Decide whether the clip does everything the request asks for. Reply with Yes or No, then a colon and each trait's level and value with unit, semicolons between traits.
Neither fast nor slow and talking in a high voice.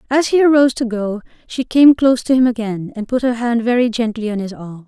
No: fast, 245 wpm; high, 235 Hz